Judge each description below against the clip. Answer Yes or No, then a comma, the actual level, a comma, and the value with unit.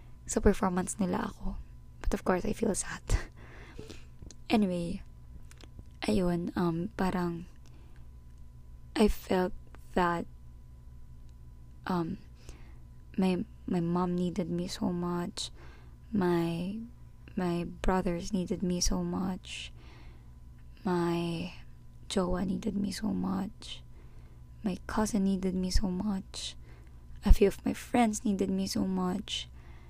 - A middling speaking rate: No, slow, 105 wpm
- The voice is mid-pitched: Yes, medium, 175 Hz